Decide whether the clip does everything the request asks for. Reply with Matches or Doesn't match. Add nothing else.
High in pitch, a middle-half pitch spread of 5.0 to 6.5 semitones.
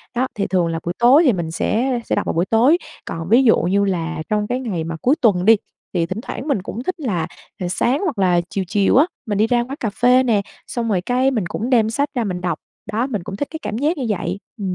Matches